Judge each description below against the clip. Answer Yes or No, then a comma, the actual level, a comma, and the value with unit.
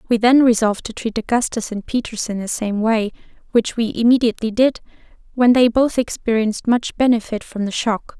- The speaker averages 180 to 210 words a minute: Yes, average, 185 wpm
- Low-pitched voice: No, high, 230 Hz